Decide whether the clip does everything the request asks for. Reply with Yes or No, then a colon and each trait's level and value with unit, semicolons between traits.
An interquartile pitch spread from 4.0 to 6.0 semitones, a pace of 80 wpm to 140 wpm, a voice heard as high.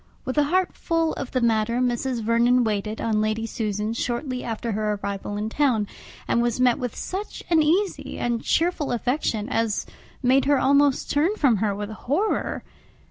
No: average, 4.6 semitones; average, 175 wpm; high, 240 Hz